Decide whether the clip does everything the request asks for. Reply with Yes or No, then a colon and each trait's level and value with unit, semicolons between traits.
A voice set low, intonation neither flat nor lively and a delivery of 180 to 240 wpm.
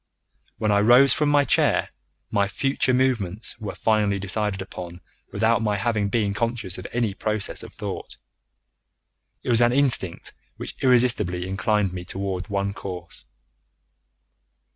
No: low, 105 Hz; average, 3.5 semitones; average, 140 wpm